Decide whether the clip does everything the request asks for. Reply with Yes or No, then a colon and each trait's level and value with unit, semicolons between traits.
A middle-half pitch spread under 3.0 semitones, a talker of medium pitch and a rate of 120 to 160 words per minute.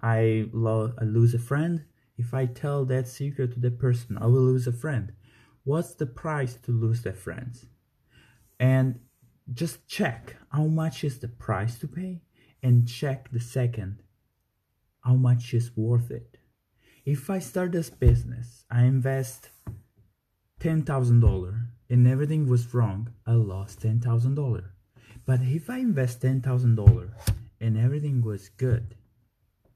No: narrow, 2.6 semitones; low, 120 Hz; average, 140 wpm